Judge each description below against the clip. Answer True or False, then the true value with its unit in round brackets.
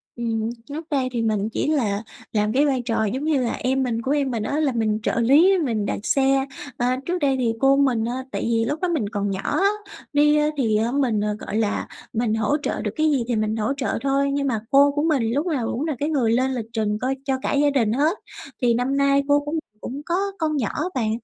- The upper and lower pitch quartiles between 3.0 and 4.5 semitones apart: True (4.2 semitones)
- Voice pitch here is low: False (260 Hz)